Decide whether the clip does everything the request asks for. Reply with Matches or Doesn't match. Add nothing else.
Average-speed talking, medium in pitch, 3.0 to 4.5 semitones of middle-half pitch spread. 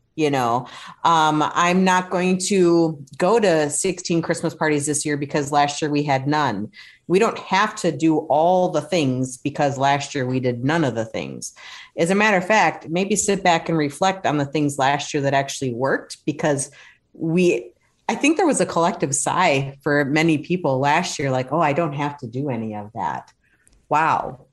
Matches